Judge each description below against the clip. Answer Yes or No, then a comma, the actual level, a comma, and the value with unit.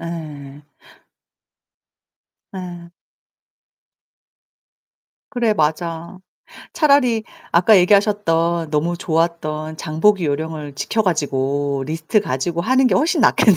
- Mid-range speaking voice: Yes, medium, 170 Hz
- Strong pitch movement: No, average, 4.9 semitones